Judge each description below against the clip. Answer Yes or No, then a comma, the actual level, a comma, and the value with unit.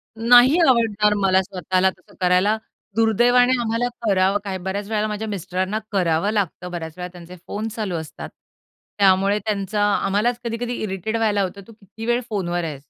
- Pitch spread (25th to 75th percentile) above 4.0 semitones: No, average, 3.0 semitones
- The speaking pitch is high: Yes, high, 205 Hz